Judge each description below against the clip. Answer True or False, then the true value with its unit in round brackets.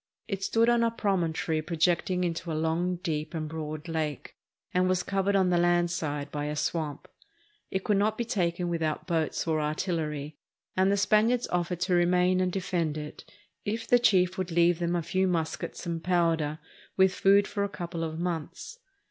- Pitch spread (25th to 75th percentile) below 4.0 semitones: True (2.9 semitones)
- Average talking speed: True (190 wpm)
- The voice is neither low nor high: True (175 Hz)